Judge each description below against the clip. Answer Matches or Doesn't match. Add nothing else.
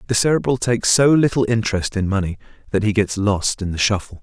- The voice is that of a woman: Doesn't match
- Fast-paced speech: Matches